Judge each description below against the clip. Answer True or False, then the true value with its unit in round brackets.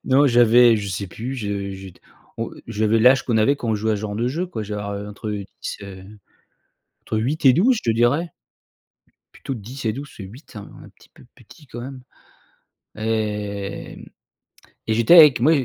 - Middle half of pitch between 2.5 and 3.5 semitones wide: False (4.2 semitones)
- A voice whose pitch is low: True (110 Hz)